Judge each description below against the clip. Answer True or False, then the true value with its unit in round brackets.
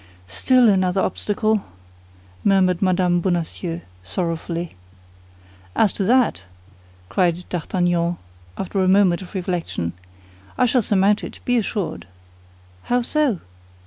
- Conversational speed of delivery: False (110 wpm)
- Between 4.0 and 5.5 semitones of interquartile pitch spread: False (3.2 semitones)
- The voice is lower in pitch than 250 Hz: True (185 Hz)